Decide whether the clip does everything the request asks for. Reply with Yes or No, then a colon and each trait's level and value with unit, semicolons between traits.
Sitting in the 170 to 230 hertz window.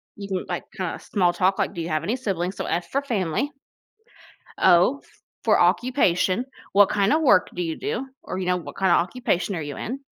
Yes: high, 190 Hz